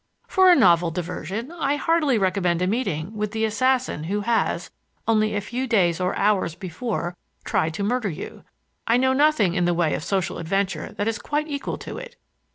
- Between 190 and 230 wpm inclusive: Yes, average, 195 wpm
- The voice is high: Yes, high, 210 Hz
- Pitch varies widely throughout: Yes, wide, 6.2 semitones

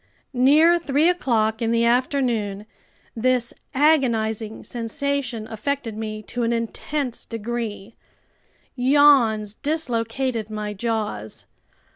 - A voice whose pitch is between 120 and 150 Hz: No, high, 235 Hz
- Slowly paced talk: Yes, slow, 95 wpm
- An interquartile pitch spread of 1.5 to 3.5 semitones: No, average, 3.9 semitones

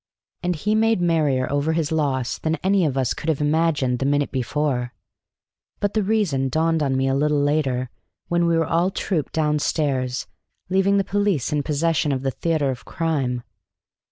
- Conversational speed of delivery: Yes, average, 180 wpm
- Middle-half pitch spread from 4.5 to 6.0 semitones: No, average, 3.8 semitones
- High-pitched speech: No, medium, 150 Hz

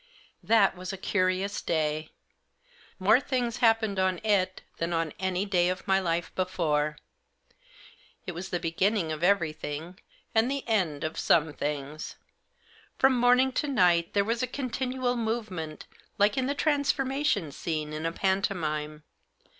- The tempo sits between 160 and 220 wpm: No, average, 140 wpm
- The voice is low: No, medium, 185 Hz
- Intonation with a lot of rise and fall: Yes, wide, 5.7 semitones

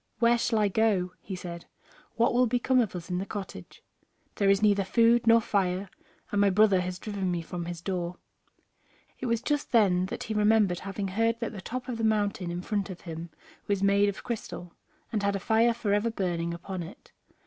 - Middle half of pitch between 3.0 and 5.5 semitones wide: Yes, average, 3.7 semitones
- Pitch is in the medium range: No, high, 200 Hz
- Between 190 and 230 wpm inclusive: Yes, fast, 205 wpm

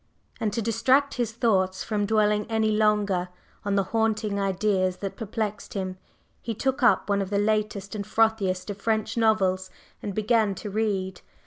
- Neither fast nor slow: Yes, average, 165 wpm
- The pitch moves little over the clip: Yes, narrow, 2.1 semitones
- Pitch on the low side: No, high, 210 Hz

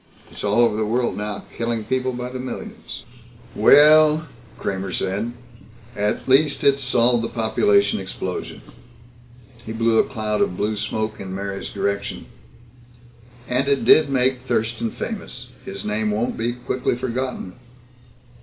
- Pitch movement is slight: No, average, 3.5 semitones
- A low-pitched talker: Yes, low, 115 Hz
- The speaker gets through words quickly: No, average, 140 wpm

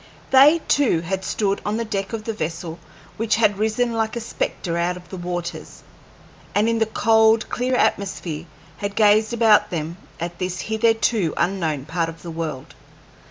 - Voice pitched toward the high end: Yes, high, 200 Hz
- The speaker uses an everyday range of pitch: Yes, average, 4.5 semitones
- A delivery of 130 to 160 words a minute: No, average, 170 wpm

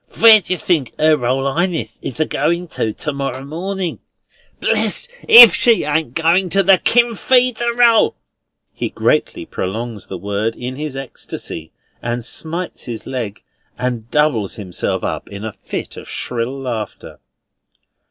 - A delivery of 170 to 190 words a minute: No, average, 160 wpm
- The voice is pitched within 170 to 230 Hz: No, medium, 140 Hz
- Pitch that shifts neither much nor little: No, wide, 7.6 semitones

